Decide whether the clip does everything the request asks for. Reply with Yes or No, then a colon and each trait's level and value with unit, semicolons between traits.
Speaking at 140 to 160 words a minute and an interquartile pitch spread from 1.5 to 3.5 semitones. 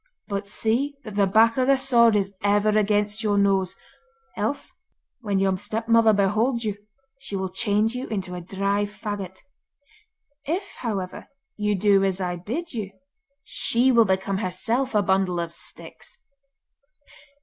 Yes: average, 150 wpm; average, 2.9 semitones